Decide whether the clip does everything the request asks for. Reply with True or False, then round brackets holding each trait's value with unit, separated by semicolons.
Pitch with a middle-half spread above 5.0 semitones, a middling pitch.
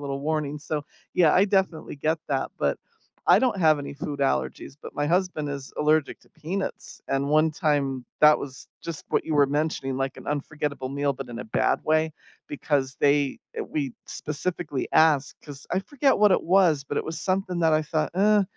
False (2.7 semitones; 150 Hz)